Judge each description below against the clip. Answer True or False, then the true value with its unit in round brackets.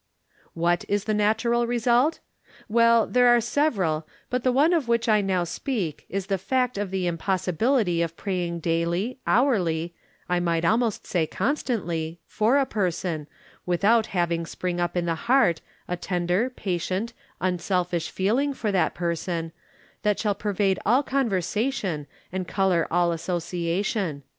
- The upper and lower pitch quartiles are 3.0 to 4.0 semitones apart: False (5.3 semitones)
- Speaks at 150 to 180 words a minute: True (155 wpm)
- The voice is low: False (190 Hz)